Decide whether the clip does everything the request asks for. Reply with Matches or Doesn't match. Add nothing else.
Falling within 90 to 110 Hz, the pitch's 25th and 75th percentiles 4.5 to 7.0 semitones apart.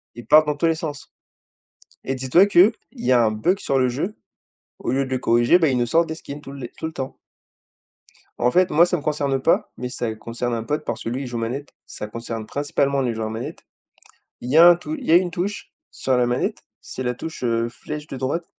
Doesn't match